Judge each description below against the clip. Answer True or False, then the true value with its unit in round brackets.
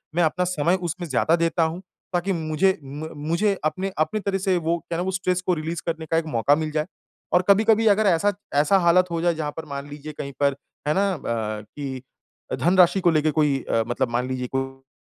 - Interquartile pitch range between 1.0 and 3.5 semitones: False (3.9 semitones)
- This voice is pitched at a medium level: True (160 Hz)